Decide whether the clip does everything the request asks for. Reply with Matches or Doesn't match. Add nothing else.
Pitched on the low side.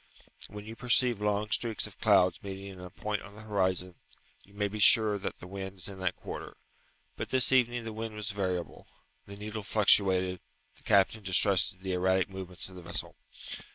Matches